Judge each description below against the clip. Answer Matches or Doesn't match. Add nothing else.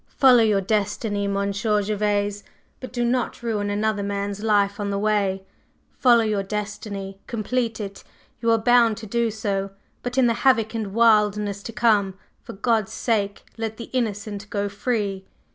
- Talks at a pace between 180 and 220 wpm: Doesn't match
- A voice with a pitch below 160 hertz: Doesn't match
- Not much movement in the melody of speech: Matches